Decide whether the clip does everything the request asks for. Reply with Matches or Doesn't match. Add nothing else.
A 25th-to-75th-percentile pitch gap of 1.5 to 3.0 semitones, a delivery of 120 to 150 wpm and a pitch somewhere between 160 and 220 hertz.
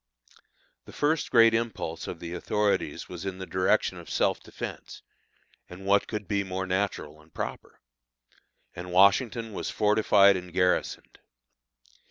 Doesn't match